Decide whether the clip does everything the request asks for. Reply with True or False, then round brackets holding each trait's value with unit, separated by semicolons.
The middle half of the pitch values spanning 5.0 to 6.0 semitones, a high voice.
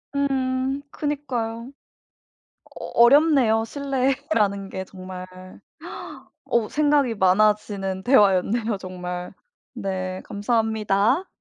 True (5.6 semitones; 225 Hz)